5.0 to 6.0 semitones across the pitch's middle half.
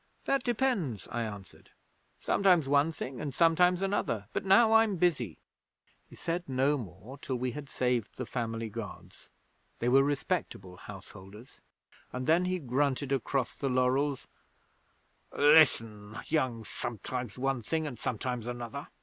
Yes: wide, 5.5 semitones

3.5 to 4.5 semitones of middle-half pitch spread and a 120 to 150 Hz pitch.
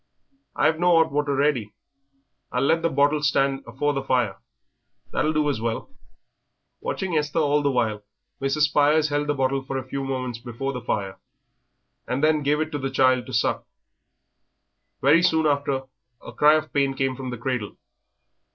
No: narrow, 2.4 semitones; medium, 140 Hz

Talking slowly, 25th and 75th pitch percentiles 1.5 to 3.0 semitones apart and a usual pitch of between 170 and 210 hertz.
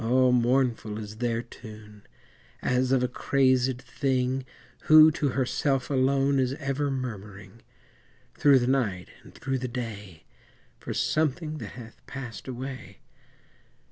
No: slow, 125 wpm; average, 2.7 semitones; low, 130 Hz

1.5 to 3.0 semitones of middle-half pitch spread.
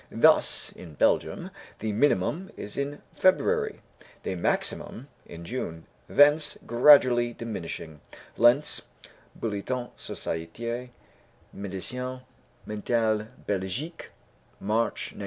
No: average, 5.3 semitones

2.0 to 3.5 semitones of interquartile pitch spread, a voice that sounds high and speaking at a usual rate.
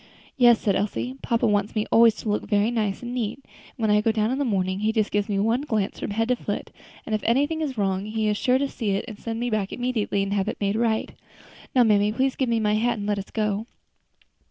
No: narrow, 2.6 semitones; high, 220 Hz; fast, 260 wpm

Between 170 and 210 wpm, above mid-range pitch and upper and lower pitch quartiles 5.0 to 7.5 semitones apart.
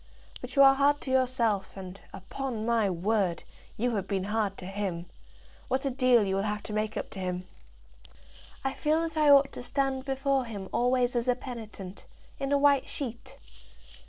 Yes: average, 190 wpm; high, 235 Hz; average, 5.3 semitones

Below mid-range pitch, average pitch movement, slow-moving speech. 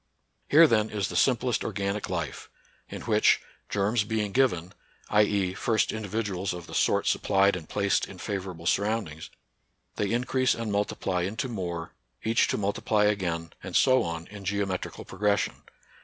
No: low, 100 Hz; average, 3.2 semitones; average, 170 wpm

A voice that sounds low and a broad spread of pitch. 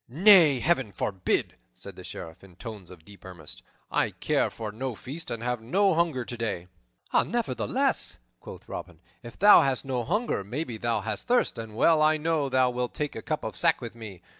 Yes: low, 120 Hz; wide, 6.4 semitones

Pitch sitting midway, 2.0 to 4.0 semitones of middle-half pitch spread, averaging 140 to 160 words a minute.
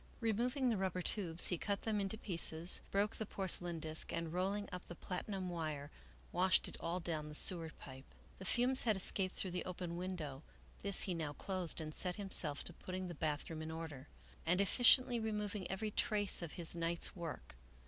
No: medium, 180 Hz; average, 3.5 semitones; average, 190 wpm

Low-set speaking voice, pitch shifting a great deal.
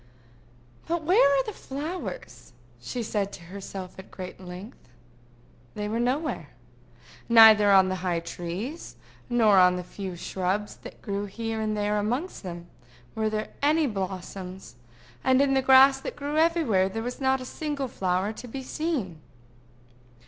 No: high, 215 Hz; wide, 6.1 semitones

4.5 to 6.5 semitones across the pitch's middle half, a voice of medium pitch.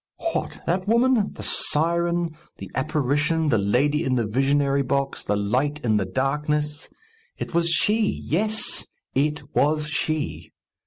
No: average, 3.6 semitones; medium, 150 Hz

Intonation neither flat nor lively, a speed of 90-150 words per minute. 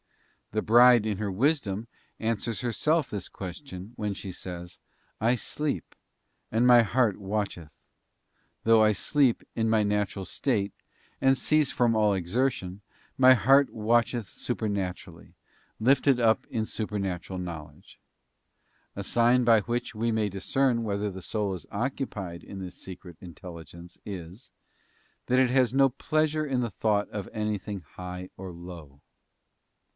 Yes: average, 4.4 semitones; average, 140 wpm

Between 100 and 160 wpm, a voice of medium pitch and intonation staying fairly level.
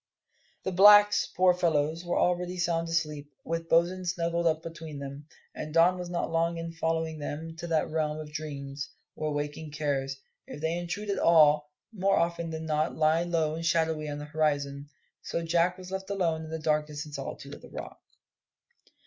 No: average, 185 wpm; medium, 160 Hz; narrow, 2.2 semitones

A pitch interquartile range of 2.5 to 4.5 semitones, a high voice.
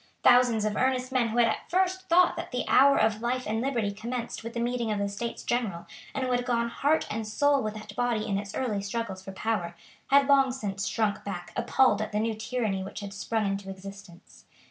Yes: average, 3.7 semitones; high, 225 Hz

